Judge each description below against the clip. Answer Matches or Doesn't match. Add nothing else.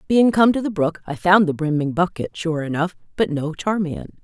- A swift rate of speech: Matches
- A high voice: Doesn't match